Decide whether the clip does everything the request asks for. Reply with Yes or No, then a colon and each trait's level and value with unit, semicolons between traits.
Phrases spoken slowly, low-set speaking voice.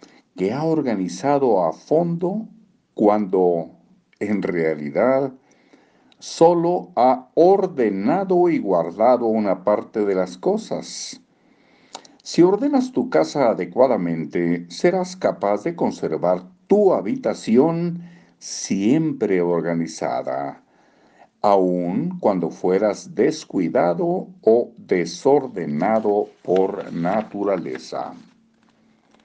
Yes: slow, 80 wpm; low, 125 Hz